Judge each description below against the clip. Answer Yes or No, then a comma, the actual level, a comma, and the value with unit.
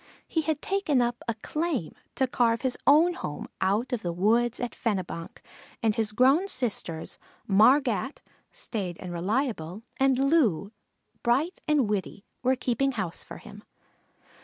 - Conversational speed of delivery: Yes, average, 145 wpm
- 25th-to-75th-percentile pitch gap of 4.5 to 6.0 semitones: Yes, average, 5.3 semitones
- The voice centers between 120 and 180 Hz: No, high, 240 Hz